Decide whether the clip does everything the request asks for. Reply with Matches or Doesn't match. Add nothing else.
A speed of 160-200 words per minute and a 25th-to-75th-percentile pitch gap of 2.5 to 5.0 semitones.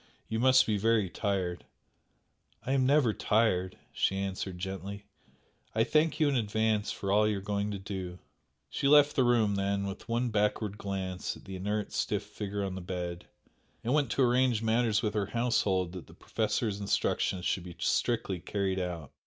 Matches